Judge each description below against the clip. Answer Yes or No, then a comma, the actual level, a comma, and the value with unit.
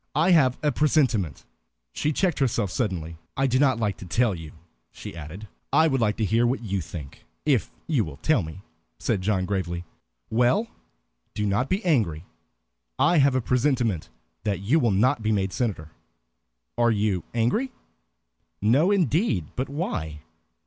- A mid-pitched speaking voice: No, low, 115 Hz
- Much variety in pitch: Yes, wide, 6.5 semitones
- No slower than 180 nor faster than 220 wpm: No, average, 165 wpm